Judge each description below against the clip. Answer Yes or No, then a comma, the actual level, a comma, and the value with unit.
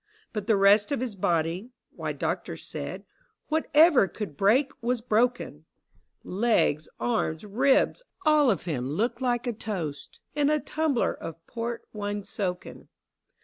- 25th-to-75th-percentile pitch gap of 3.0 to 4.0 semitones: No, average, 5.0 semitones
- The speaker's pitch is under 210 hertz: No, high, 220 Hz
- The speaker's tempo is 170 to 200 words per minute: No, average, 160 wpm